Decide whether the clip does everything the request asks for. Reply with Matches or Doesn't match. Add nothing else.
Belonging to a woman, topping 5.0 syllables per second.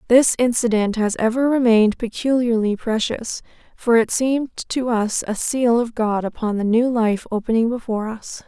Doesn't match